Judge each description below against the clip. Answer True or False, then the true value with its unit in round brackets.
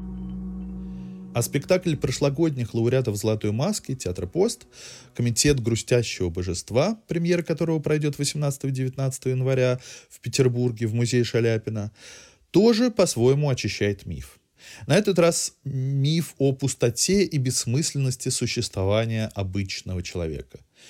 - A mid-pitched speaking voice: False (130 Hz)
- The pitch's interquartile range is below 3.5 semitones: False (5.1 semitones)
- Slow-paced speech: True (105 wpm)